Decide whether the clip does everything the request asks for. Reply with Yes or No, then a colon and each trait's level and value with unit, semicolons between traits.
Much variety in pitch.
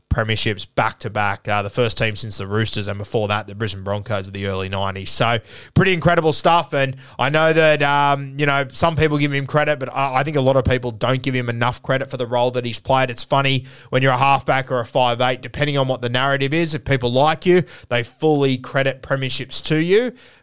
No: average, 3.6 semitones